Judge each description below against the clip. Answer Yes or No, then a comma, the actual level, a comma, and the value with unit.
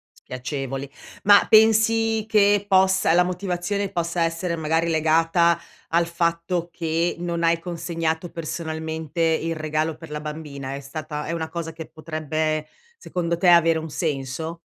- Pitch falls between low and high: Yes, medium, 165 Hz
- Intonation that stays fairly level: Yes, narrow, 1.9 semitones